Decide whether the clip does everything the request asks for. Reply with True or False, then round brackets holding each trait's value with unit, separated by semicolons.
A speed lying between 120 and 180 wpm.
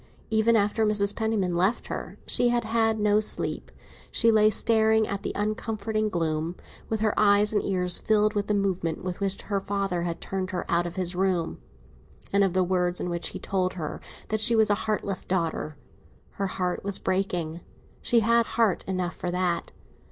False (190 wpm)